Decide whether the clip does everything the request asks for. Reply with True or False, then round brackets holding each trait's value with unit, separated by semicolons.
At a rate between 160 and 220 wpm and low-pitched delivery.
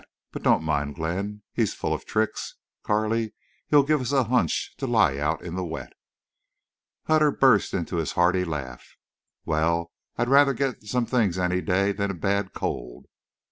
True (170 wpm; 100 Hz)